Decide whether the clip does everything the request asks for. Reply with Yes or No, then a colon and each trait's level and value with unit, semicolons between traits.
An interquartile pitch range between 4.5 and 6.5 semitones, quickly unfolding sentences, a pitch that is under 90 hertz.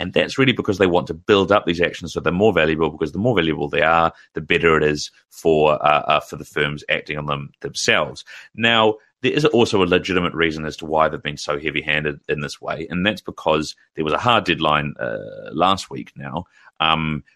No: average, 3.4 semitones; fast, 225 wpm; very low, 80 Hz